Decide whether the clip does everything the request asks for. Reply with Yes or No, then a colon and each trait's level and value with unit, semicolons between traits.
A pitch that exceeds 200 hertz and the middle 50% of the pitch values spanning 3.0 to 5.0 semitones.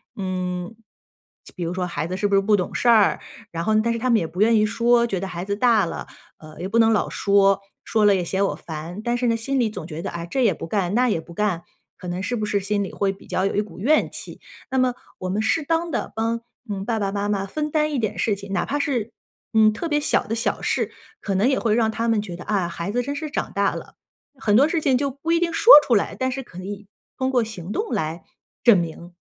Yes: high, 210 Hz; average, 4.2 semitones